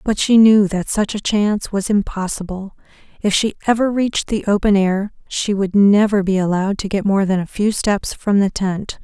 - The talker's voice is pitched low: No, high, 200 Hz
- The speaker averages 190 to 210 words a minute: Yes, fast, 205 wpm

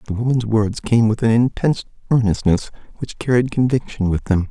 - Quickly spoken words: No, average, 175 wpm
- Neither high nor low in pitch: No, low, 115 Hz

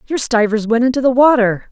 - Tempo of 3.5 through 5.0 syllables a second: No, 5.8 syllables/s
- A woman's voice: Yes, female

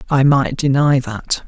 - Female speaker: No, male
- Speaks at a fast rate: No, average, 165 wpm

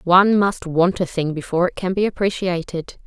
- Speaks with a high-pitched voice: No, medium, 180 Hz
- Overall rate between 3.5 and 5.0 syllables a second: No, 5.5 syllables/s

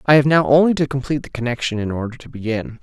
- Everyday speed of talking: No, fast, 255 wpm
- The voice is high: No, low, 130 Hz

